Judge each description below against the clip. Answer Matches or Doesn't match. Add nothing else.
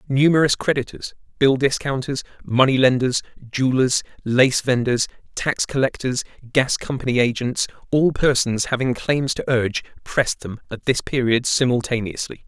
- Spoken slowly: Matches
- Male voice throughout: Matches